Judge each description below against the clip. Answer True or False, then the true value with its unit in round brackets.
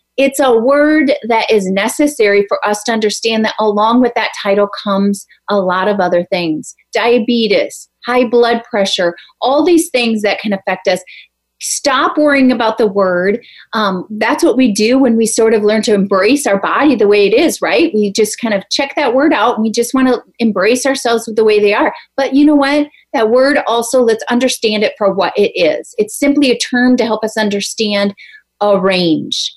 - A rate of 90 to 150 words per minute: False (205 wpm)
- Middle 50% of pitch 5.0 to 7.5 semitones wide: False (4.3 semitones)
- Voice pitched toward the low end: False (225 Hz)